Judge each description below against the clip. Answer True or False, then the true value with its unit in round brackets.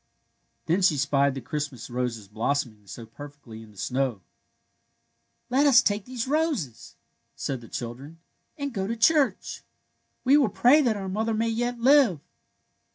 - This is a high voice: False (160 Hz)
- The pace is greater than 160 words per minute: True (170 wpm)